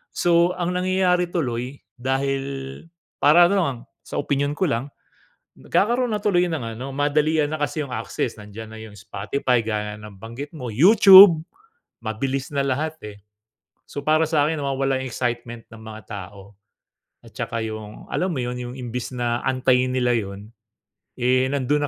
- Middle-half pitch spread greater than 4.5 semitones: Yes, average, 5.0 semitones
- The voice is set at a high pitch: No, low, 130 Hz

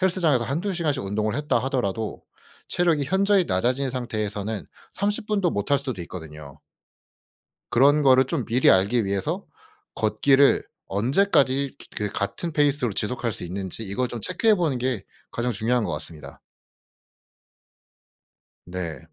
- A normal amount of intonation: No, wide, 6.3 semitones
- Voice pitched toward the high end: No, low, 125 Hz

